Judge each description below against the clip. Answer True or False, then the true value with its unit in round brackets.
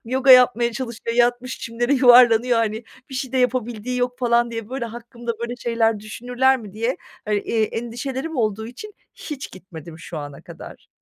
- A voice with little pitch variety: True (2.0 semitones)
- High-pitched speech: True (240 Hz)